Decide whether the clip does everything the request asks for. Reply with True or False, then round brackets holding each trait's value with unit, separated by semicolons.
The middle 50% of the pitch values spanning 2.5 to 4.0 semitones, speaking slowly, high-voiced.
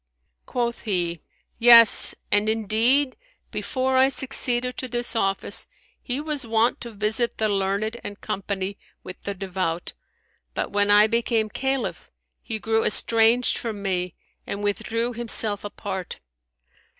True (3.1 semitones; 130 wpm; 220 Hz)